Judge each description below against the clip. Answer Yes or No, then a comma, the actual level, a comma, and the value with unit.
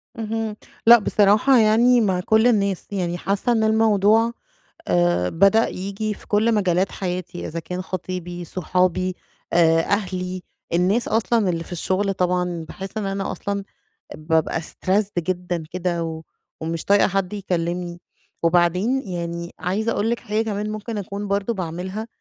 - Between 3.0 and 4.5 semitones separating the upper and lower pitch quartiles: Yes, average, 3.3 semitones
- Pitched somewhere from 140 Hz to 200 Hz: Yes, high, 190 Hz